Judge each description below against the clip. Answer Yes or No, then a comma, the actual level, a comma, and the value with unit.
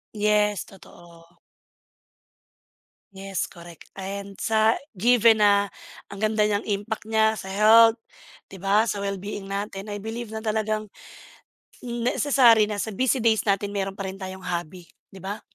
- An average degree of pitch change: No, narrow, 2.1 semitones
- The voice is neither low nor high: No, high, 205 Hz